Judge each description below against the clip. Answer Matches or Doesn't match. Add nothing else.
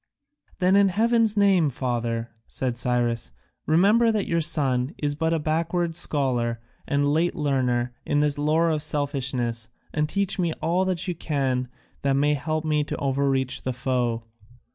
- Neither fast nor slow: Matches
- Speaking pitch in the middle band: Matches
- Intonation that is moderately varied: Matches